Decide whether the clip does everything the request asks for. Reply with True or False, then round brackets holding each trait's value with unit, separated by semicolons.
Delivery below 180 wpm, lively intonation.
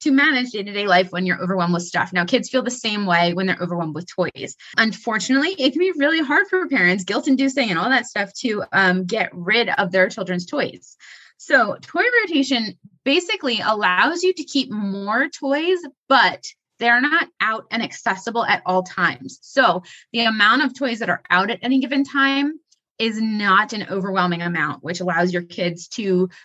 False (195 wpm; 6.9 semitones)